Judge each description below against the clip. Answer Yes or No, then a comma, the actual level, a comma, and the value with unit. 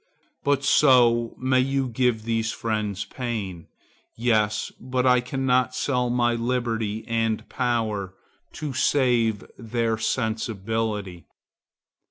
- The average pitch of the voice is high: No, low, 115 Hz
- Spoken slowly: Yes, slow, 110 wpm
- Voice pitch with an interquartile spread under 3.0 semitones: Yes, narrow, 2.4 semitones